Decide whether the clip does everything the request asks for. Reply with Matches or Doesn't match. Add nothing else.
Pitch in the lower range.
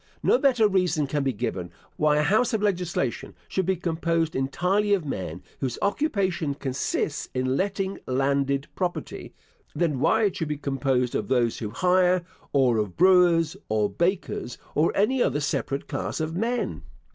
Doesn't match